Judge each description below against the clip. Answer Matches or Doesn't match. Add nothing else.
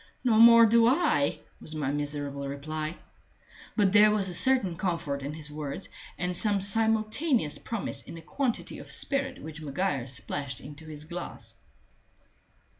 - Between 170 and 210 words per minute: Doesn't match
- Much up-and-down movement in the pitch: Matches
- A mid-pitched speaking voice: Matches